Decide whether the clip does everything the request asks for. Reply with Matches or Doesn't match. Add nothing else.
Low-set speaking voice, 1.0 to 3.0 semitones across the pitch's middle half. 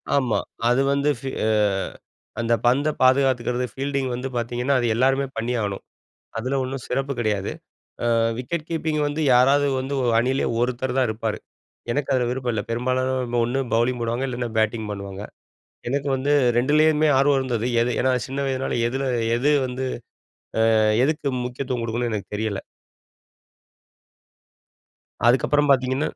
Matches